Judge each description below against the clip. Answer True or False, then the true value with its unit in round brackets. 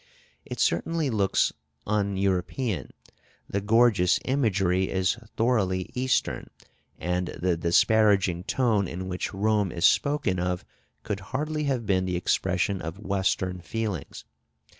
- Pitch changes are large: False (3.6 semitones)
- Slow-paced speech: True (120 wpm)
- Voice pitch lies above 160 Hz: False (95 Hz)